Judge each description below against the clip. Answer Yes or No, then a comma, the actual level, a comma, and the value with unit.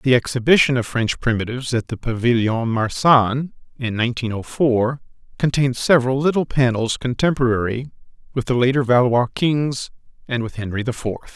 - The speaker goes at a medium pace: Yes, average, 150 wpm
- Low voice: Yes, low, 125 Hz